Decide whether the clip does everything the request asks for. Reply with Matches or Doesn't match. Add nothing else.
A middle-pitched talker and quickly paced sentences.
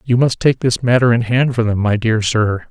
Doesn't match